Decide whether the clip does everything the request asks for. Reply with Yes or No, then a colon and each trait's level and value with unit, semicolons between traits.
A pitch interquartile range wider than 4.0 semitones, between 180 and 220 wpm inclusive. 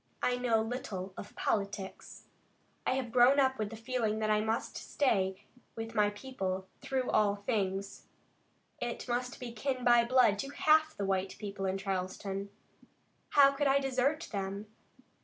No: average, 4.4 semitones; average, 160 wpm